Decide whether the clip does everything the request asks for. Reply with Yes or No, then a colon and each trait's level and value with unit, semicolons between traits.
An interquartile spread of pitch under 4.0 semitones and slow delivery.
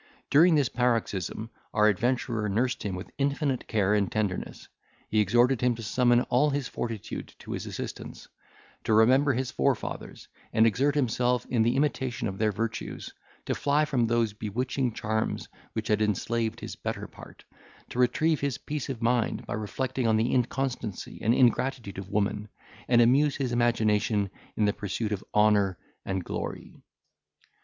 No: average, 3.3 semitones; average, 160 wpm